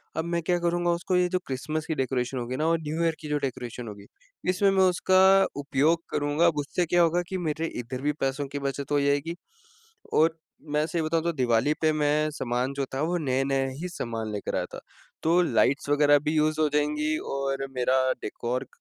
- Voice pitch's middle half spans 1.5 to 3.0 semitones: No, average, 3.6 semitones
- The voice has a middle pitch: Yes, medium, 150 Hz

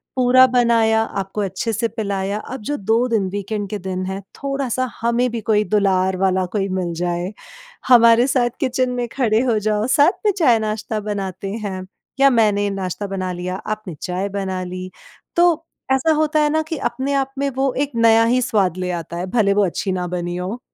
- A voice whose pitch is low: No, high, 215 Hz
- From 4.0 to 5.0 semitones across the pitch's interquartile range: Yes, average, 4.7 semitones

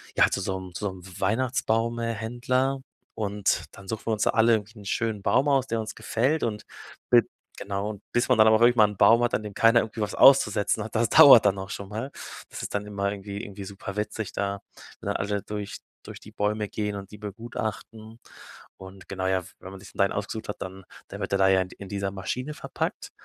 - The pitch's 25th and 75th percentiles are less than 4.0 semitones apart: Yes, narrow, 2.5 semitones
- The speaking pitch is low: Yes, low, 105 Hz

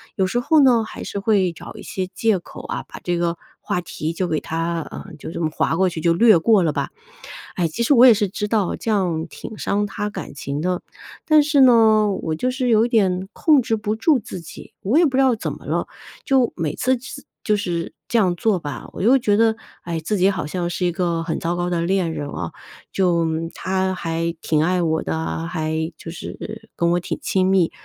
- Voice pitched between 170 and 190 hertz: Yes, medium, 185 Hz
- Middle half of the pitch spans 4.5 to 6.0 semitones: Yes, average, 4.8 semitones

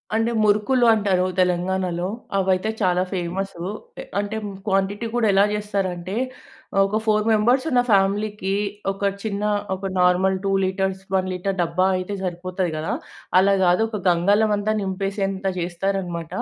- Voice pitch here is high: Yes, high, 195 Hz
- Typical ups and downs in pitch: No, narrow, 2.1 semitones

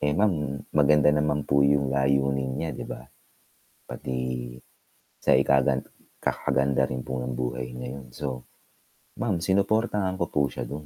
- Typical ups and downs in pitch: No, narrow, 2.1 semitones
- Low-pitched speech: Yes, very low, 70 Hz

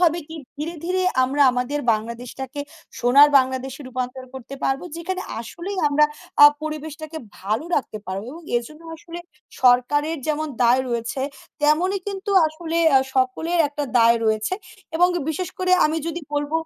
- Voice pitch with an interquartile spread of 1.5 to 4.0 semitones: No, average, 4.6 semitones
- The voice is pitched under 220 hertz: No, very high, 290 Hz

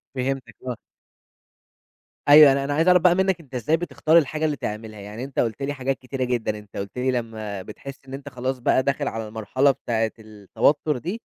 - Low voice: Yes, low, 130 Hz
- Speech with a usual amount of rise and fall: Yes, average, 4.4 semitones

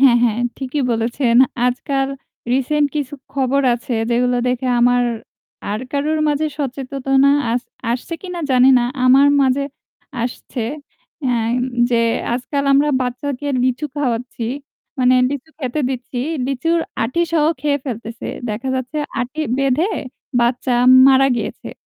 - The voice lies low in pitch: No, very high, 260 Hz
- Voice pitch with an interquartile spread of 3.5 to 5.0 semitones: No, narrow, 2.5 semitones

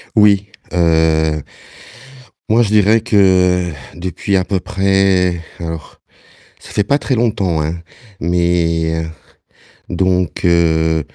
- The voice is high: No, very low, 90 Hz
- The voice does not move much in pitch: No, average, 3.0 semitones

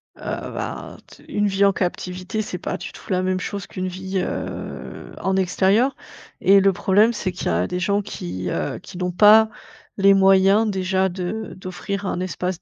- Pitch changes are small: Yes, narrow, 1.7 semitones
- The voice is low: No, high, 190 Hz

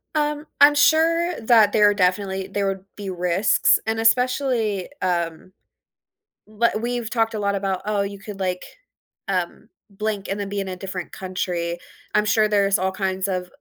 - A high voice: Yes, high, 200 Hz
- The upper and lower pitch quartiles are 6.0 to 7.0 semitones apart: No, average, 2.9 semitones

